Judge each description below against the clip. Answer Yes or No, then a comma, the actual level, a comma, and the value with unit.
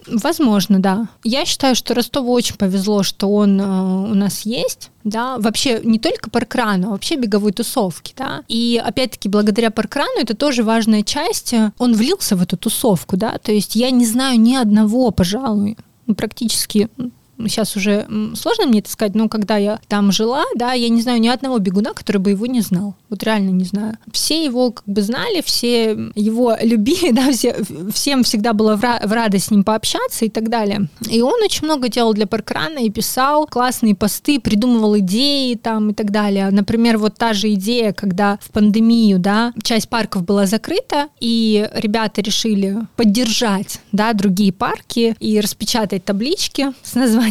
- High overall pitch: Yes, high, 225 Hz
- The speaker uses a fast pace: Yes, fast, 175 wpm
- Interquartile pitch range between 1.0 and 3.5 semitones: Yes, narrow, 2.6 semitones